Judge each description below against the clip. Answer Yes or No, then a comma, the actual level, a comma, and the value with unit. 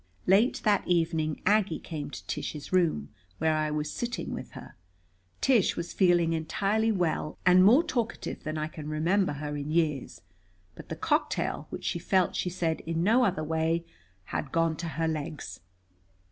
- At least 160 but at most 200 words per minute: Yes, average, 170 wpm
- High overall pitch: No, medium, 165 Hz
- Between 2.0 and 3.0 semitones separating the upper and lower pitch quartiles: No, average, 3.4 semitones